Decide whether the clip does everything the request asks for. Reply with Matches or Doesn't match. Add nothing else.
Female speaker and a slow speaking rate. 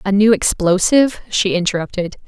Matches